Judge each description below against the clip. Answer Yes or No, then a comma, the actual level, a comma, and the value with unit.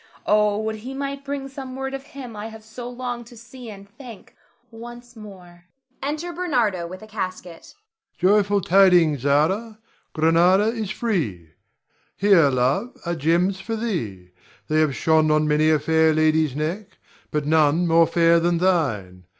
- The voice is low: No, high, 190 Hz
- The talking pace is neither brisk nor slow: Yes, average, 160 wpm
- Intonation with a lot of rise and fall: Yes, wide, 6.4 semitones